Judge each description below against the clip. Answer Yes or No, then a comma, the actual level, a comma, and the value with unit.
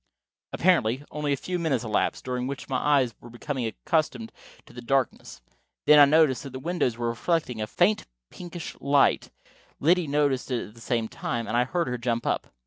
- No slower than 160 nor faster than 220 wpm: Yes, average, 195 wpm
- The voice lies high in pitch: No, low, 130 Hz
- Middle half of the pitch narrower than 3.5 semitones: No, average, 4.1 semitones